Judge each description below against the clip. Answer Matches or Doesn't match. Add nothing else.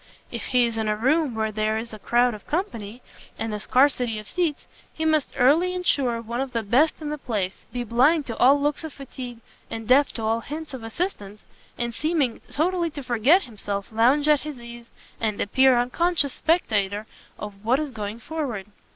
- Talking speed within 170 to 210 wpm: Matches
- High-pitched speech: Matches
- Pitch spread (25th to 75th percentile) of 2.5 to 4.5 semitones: Doesn't match